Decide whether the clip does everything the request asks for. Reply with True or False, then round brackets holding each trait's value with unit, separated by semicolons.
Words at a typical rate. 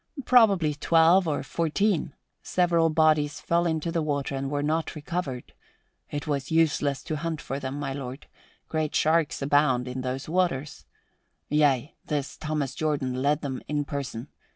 True (155 wpm)